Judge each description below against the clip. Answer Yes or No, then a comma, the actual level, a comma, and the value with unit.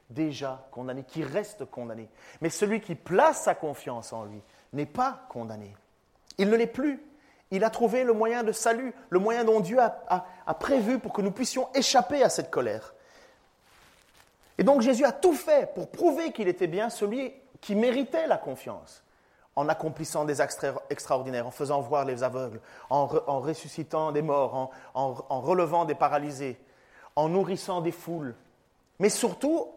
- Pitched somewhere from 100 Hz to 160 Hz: No, medium, 180 Hz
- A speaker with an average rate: Yes, average, 180 wpm